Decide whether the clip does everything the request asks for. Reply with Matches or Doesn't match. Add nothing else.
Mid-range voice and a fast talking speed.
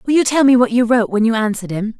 Doesn't match